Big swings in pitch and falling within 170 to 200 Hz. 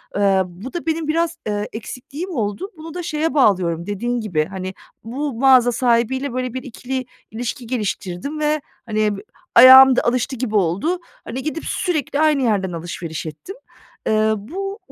No: wide, 6.5 semitones; high, 245 Hz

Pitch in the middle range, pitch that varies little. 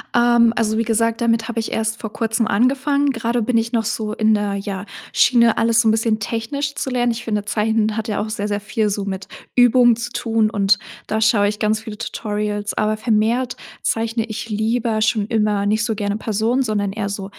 No: high, 220 Hz; narrow, 1.7 semitones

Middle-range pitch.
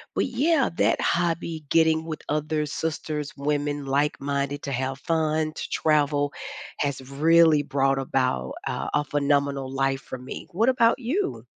Yes: medium, 150 Hz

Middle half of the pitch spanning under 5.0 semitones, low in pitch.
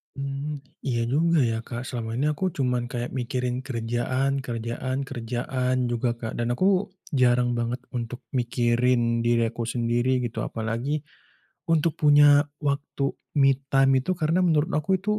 Yes: average, 2.8 semitones; low, 125 Hz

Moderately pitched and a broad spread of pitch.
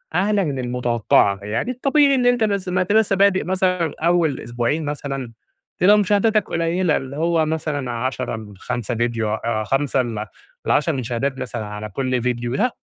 Yes: medium, 145 Hz; wide, 7.7 semitones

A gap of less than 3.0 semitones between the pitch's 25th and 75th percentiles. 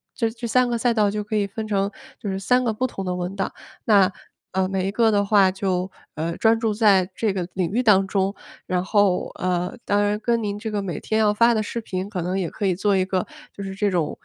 Yes: narrow, 2.6 semitones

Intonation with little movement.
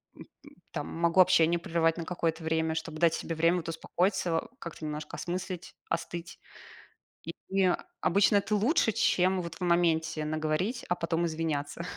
Yes: narrow, 2.0 semitones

